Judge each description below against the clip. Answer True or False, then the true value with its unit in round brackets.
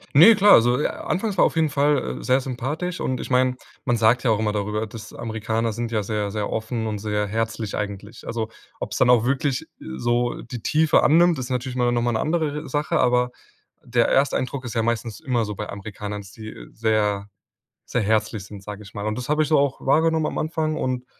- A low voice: True (120 Hz)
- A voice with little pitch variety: False (4.0 semitones)